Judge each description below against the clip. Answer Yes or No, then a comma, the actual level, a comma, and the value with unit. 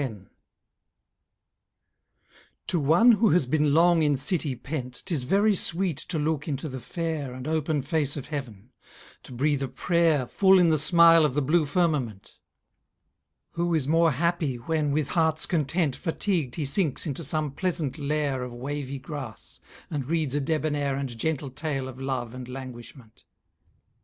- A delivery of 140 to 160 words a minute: Yes, average, 155 wpm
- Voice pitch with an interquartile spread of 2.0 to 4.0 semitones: Yes, average, 3.7 semitones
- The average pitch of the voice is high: No, medium, 150 Hz